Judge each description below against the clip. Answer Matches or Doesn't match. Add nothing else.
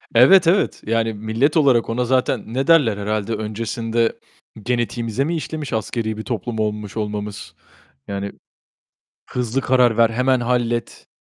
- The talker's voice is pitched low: Matches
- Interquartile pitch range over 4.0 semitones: Doesn't match